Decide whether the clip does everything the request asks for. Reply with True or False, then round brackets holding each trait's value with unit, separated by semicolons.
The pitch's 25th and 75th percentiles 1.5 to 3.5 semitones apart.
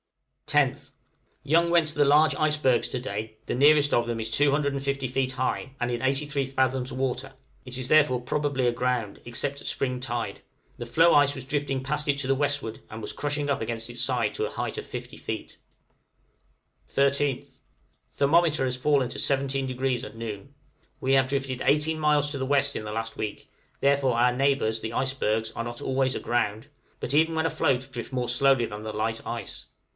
True (2.9 semitones)